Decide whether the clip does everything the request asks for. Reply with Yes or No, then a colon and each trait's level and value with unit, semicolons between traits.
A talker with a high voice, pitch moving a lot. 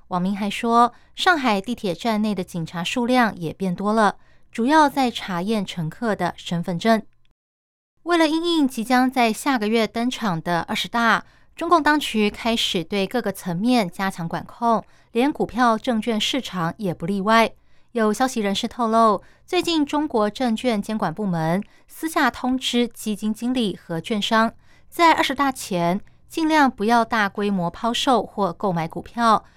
No: high, 220 Hz; average, 4.2 semitones